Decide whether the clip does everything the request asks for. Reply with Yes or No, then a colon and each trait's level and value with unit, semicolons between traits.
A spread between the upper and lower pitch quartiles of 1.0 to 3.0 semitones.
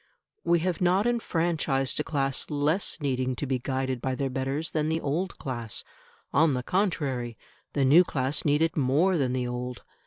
No: average, 3.9 semitones